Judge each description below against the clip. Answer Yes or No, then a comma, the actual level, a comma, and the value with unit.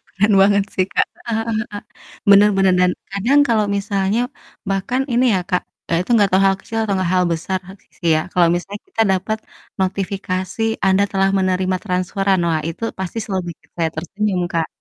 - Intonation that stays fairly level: Yes, narrow, 1.8 semitones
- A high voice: Yes, high, 195 Hz